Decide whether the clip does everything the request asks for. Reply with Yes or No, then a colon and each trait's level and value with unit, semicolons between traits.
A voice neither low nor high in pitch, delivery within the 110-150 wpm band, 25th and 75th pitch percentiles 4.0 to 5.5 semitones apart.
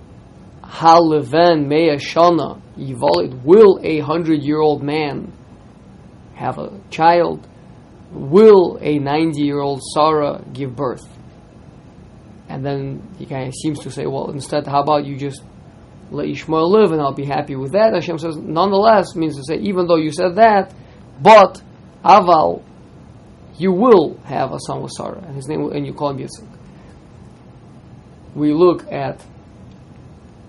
No: medium, 155 Hz; average, 140 wpm; average, 3.2 semitones